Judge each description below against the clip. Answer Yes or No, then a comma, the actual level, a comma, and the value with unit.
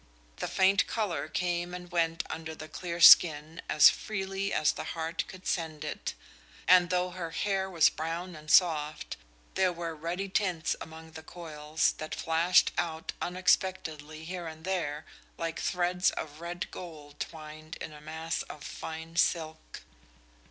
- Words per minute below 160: Yes, average, 150 wpm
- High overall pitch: No, medium, 165 Hz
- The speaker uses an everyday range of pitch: No, narrow, 2.3 semitones